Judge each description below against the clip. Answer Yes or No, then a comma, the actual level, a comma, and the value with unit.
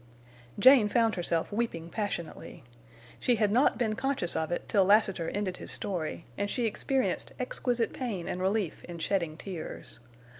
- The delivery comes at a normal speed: Yes, average, 155 wpm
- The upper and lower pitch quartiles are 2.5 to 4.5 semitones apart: No, average, 4.9 semitones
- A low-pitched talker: No, high, 205 Hz